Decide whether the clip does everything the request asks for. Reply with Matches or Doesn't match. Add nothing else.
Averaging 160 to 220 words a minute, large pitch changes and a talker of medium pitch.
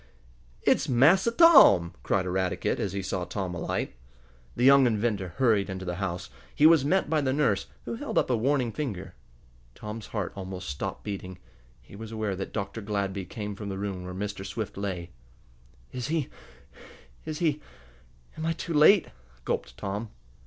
Doesn't match